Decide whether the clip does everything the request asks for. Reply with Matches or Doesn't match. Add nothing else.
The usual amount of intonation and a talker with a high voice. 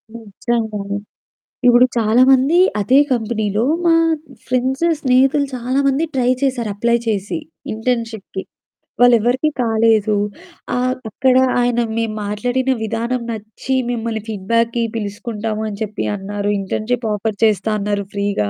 Matches